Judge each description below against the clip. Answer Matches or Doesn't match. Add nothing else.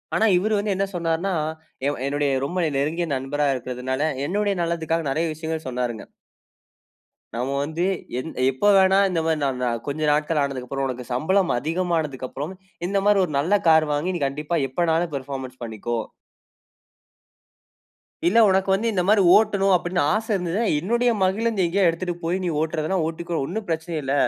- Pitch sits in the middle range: Matches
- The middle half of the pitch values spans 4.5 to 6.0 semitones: Matches